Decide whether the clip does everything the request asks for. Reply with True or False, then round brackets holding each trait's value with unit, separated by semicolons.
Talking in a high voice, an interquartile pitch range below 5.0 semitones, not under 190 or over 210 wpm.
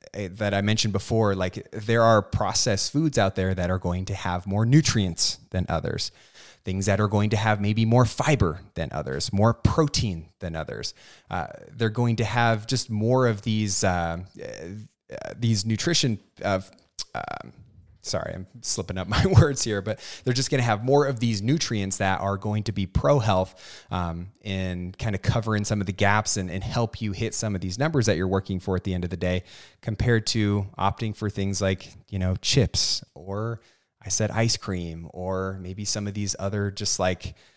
False (105 Hz; 3.2 semitones; 200 wpm)